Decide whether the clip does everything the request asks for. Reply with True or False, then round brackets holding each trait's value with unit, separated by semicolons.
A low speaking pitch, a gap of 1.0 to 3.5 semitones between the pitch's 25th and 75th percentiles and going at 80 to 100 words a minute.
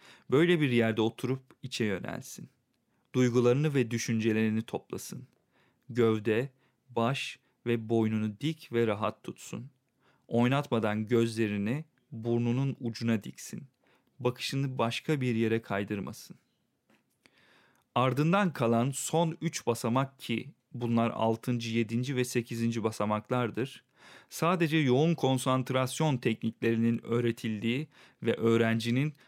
True (120 Hz; 2.5 semitones; 95 wpm)